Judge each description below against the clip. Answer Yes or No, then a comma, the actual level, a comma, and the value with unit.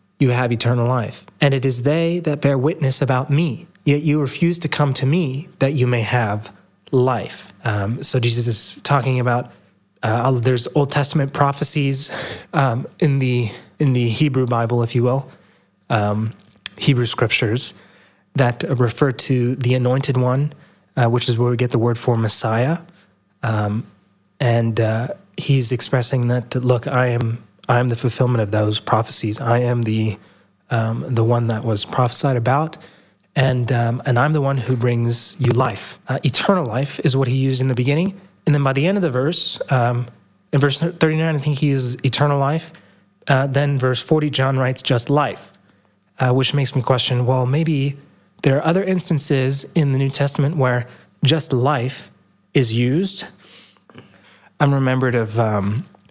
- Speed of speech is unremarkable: Yes, average, 170 wpm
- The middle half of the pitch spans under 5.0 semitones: Yes, average, 3.2 semitones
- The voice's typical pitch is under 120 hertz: No, low, 130 Hz